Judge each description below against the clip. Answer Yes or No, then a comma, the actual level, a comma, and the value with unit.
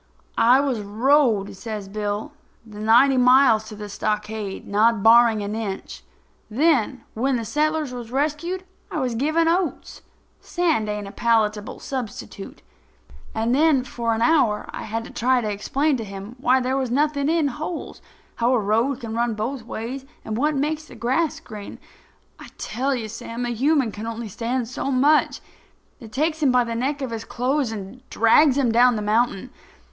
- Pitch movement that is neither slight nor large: Yes, average, 4.1 semitones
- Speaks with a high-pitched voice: Yes, high, 240 Hz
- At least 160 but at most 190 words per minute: Yes, average, 175 wpm